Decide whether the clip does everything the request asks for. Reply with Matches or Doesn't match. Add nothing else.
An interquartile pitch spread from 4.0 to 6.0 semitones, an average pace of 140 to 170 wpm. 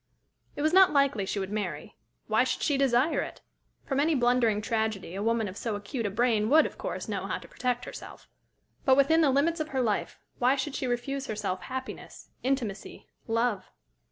Doesn't match